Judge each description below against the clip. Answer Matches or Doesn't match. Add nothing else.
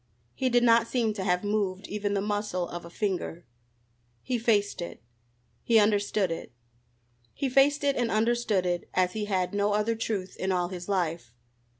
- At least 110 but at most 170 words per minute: Doesn't match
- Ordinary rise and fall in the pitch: Matches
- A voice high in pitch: Matches